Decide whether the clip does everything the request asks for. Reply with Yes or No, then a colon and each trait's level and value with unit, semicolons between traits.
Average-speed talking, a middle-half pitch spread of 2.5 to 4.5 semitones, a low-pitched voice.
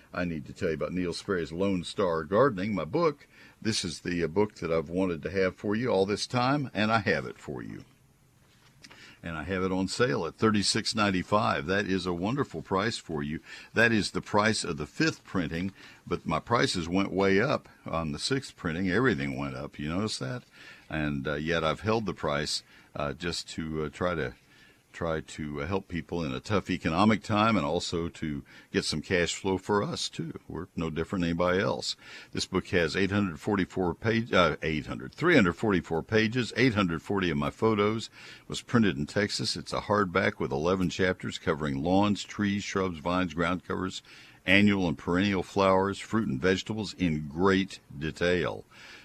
Yes: average, 185 wpm; average, 3.9 semitones; very low, 95 Hz